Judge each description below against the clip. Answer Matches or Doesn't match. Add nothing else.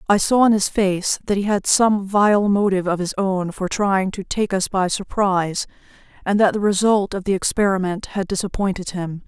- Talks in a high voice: Matches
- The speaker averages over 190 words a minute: Matches